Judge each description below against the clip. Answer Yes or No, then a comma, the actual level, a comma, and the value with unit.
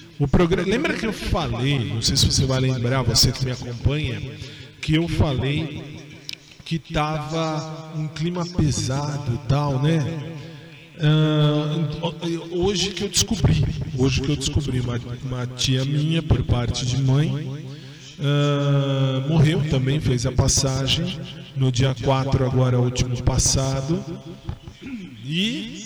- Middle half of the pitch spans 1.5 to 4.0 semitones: Yes, average, 3.1 semitones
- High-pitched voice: No, medium, 140 Hz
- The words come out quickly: No, average, 135 wpm